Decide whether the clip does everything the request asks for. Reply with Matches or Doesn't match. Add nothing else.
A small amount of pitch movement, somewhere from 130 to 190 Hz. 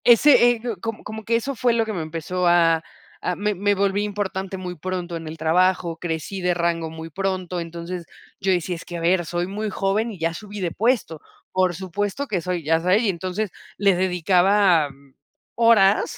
Doesn't match